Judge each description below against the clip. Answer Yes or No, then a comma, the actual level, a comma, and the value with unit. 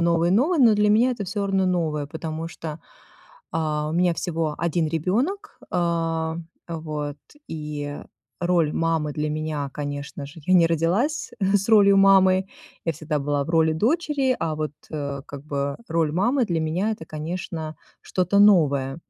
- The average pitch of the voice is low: No, medium, 165 Hz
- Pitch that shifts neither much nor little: Yes, average, 4.1 semitones